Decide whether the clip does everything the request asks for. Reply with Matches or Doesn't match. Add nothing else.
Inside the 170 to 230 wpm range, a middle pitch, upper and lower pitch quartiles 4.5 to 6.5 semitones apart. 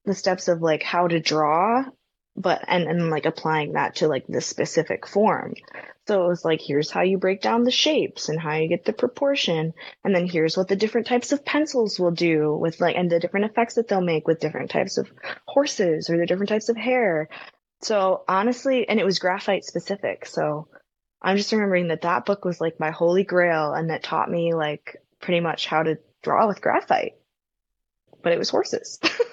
Matches